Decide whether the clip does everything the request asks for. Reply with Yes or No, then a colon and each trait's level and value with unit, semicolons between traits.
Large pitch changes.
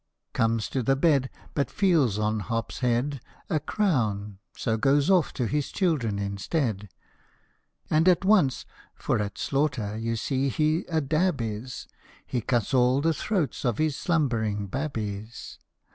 Yes: wide, 5.7 semitones